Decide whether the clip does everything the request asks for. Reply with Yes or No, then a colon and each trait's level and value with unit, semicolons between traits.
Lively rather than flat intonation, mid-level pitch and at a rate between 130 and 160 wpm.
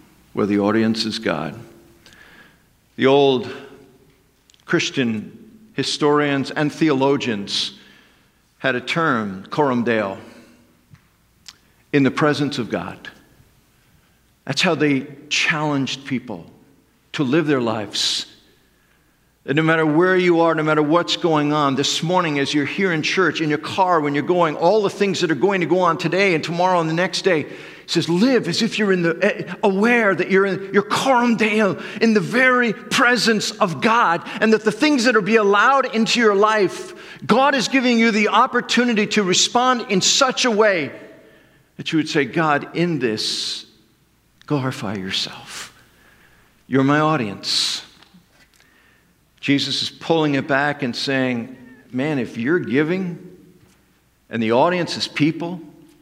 Yes: wide, 7.1 semitones; medium, 165 Hz; average, 150 wpm